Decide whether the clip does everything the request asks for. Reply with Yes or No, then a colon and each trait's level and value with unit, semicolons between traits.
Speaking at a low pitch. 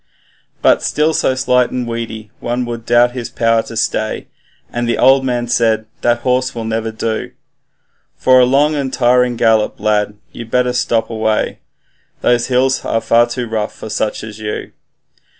Yes: low, 120 Hz